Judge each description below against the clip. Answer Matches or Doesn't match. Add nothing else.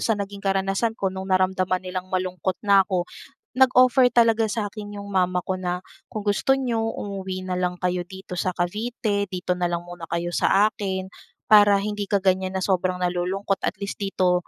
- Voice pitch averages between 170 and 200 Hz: Matches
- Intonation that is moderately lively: Doesn't match